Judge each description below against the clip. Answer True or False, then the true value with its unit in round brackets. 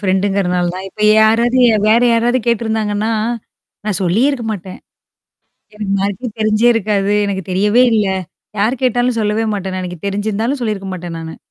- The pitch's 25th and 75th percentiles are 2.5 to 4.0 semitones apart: True (2.9 semitones)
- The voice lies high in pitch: True (210 Hz)